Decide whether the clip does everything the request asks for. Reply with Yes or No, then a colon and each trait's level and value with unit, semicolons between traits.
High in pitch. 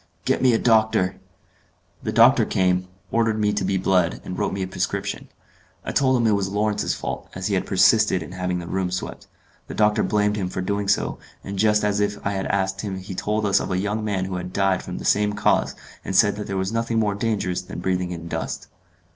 No: low, 100 Hz